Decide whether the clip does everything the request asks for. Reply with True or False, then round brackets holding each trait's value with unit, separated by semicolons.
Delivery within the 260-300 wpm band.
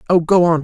True (285 wpm)